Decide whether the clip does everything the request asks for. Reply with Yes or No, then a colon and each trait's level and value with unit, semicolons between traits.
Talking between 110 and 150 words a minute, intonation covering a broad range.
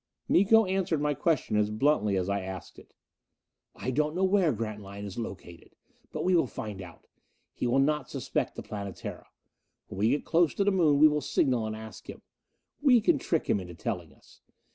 No: average, 195 wpm; wide, 8.4 semitones